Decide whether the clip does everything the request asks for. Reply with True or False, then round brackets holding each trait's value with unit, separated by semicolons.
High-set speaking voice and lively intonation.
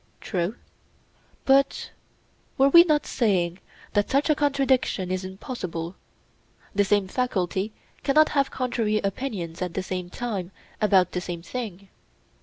True (205 Hz; 6.2 semitones)